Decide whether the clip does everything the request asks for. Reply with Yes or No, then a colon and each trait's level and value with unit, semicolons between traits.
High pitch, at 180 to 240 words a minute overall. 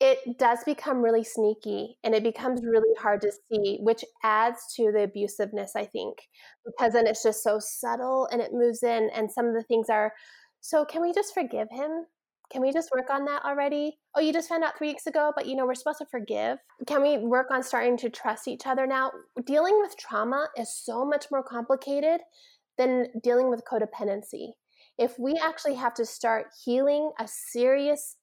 Yes: very high, 255 Hz; average, 200 wpm